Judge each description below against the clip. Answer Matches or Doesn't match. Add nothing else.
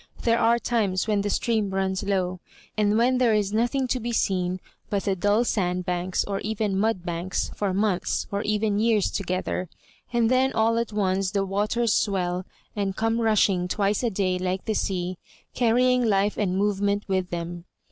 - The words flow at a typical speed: Matches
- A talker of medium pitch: Doesn't match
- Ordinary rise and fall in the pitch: Matches